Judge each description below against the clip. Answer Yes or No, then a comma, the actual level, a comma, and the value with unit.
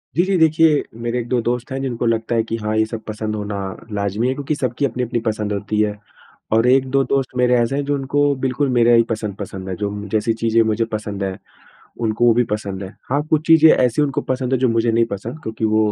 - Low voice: Yes, low, 115 Hz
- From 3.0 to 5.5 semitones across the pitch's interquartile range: Yes, average, 3.5 semitones